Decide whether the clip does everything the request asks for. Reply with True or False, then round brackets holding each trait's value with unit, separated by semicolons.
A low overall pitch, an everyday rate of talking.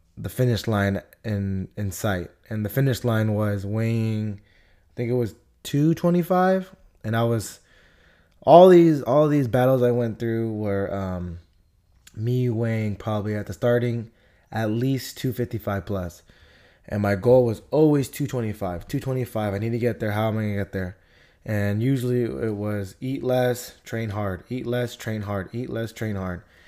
True (110 Hz; 165 wpm)